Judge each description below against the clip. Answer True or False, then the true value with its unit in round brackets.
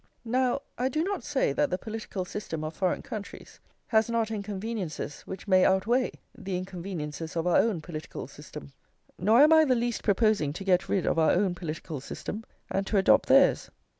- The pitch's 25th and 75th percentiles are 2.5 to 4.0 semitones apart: False (4.6 semitones)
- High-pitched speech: True (195 Hz)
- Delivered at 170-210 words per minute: True (185 wpm)